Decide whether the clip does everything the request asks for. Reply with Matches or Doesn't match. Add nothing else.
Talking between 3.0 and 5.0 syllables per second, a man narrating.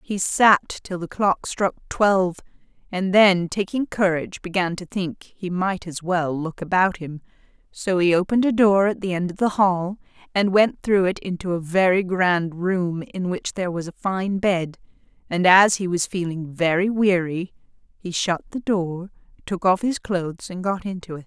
Doesn't match